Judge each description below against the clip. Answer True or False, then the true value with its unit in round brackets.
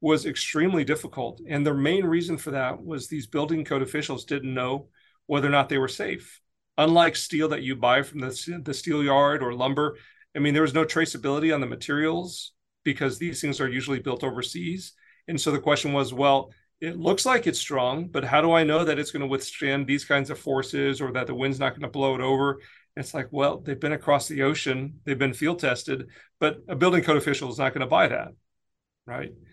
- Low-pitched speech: False (145 Hz)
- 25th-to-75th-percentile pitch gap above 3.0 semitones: False (2.4 semitones)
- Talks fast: True (225 wpm)